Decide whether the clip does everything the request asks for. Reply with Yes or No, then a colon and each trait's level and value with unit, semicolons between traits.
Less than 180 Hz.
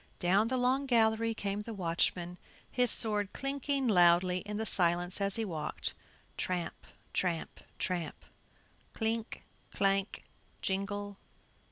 No: high, 200 Hz